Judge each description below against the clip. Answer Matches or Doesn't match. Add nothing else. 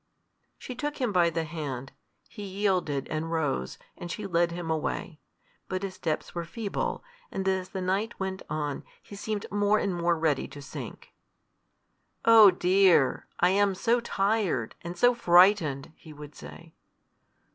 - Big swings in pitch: Doesn't match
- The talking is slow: Doesn't match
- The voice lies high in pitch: Doesn't match